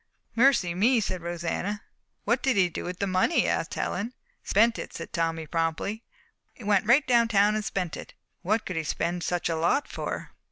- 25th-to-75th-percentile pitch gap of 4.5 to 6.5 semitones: Yes, average, 4.9 semitones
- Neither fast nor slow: Yes, average, 190 wpm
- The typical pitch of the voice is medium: No, high, 200 Hz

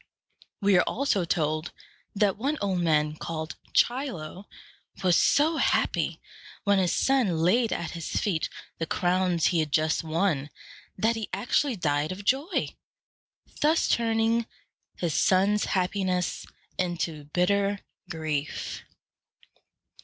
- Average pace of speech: No, slow, 120 wpm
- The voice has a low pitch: No, medium, 185 Hz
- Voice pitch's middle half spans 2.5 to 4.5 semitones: No, average, 4.9 semitones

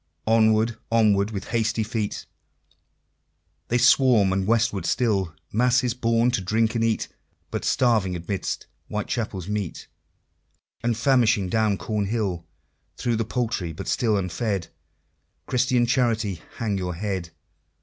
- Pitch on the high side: No, low, 110 Hz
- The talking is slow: Yes, slow, 120 wpm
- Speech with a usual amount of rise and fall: Yes, average, 3.0 semitones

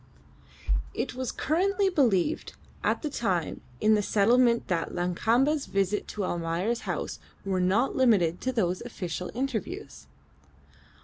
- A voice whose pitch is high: Yes, high, 220 Hz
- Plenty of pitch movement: Yes, wide, 6.0 semitones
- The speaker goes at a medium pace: No, slow, 125 wpm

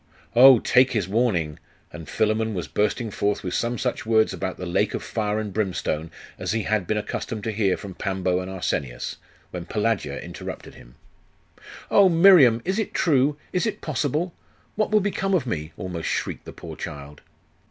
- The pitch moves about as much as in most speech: No, wide, 6.0 semitones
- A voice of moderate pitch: No, low, 110 Hz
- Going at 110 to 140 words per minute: No, average, 180 wpm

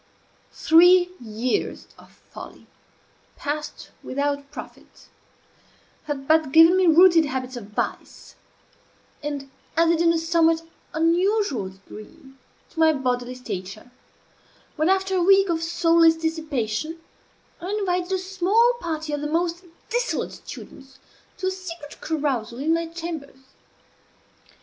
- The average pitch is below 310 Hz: No, very high, 320 Hz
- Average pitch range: Yes, average, 4.2 semitones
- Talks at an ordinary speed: No, slow, 120 wpm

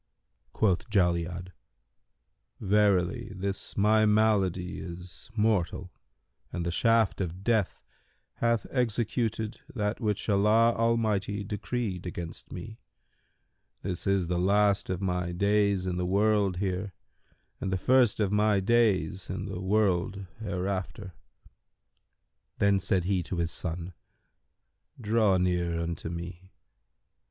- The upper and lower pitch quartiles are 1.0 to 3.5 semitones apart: Yes, average, 3.1 semitones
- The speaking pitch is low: Yes, low, 100 Hz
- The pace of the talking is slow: Yes, slow, 115 wpm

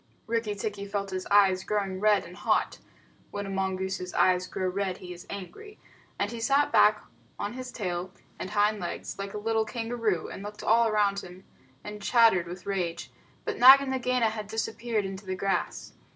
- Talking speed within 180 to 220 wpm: Yes, average, 185 wpm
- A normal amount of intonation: Yes, average, 3.0 semitones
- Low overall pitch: No, high, 205 Hz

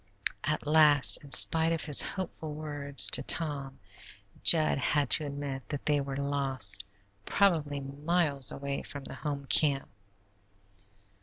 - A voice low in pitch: No, medium, 145 Hz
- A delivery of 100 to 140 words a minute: Yes, slow, 135 wpm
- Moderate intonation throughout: No, narrow, 1.9 semitones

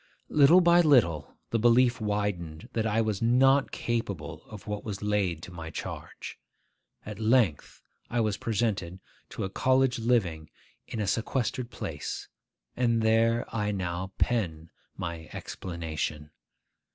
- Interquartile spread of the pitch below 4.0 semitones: No, average, 5.2 semitones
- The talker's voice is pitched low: Yes, low, 105 Hz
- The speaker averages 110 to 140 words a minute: Yes, slow, 135 wpm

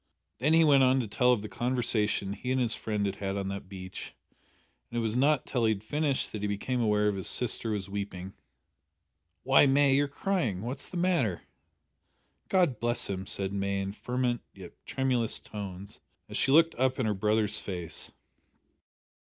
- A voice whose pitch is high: No, low, 110 Hz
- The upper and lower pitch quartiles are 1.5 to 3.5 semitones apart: No, average, 4.9 semitones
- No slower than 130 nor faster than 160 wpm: No, average, 185 wpm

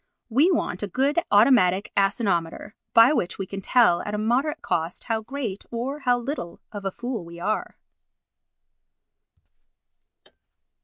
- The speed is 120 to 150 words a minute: Yes, average, 140 wpm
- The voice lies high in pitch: Yes, high, 220 Hz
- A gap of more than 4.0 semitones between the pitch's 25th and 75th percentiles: Yes, average, 4.8 semitones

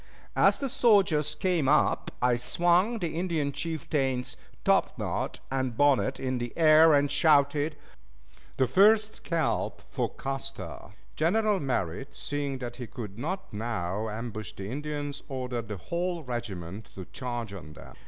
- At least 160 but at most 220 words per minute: No, average, 140 wpm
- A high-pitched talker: No, low, 135 Hz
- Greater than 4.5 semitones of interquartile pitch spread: Yes, average, 5.2 semitones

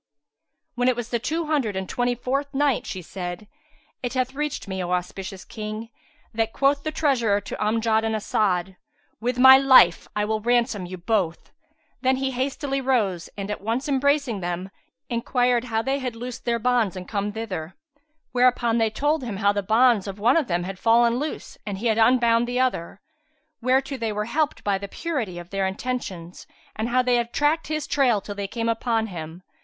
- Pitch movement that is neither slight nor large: Yes, average, 4.3 semitones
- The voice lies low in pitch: No, high, 230 Hz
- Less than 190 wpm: No, average, 195 wpm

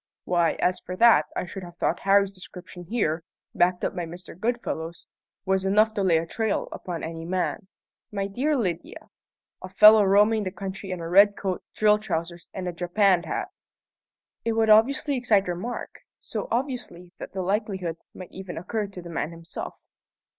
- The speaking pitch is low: No, high, 190 Hz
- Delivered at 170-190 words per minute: Yes, average, 175 wpm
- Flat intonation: No, average, 3.4 semitones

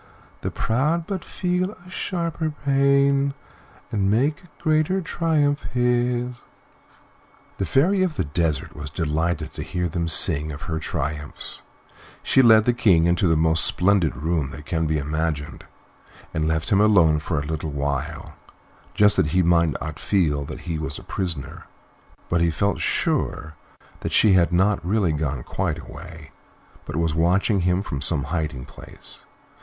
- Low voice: Yes, very low, 85 Hz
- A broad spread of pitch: Yes, wide, 7.9 semitones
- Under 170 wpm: Yes, average, 160 wpm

